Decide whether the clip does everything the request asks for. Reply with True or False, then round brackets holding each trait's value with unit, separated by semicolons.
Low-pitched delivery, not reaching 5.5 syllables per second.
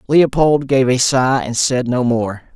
True (130 Hz; 3.9 syllables/s)